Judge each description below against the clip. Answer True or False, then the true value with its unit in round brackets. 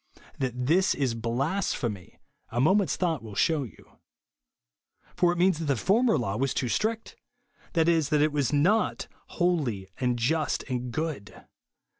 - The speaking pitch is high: False (145 Hz)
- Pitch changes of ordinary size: False (6.0 semitones)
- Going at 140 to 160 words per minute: True (155 wpm)